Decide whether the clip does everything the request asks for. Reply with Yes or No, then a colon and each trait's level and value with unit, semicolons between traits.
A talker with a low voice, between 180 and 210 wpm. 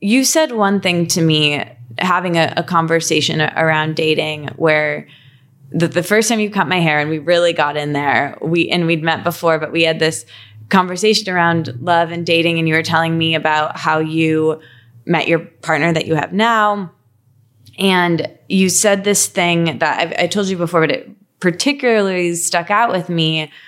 No: medium, 165 Hz; average, 190 wpm